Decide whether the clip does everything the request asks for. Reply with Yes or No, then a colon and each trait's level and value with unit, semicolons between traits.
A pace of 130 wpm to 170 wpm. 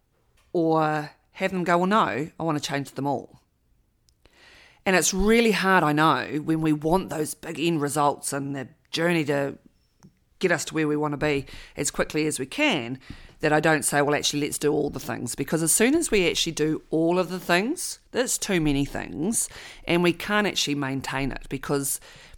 No: average, 200 wpm